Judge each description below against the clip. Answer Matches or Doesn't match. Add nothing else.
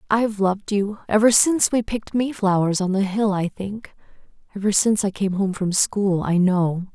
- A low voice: Doesn't match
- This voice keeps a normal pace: Matches